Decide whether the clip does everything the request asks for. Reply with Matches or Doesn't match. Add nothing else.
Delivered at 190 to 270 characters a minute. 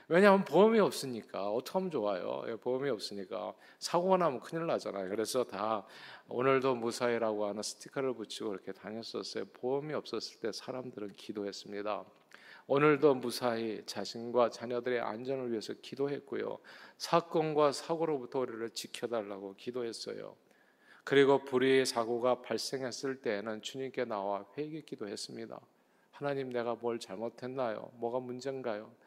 Doesn't match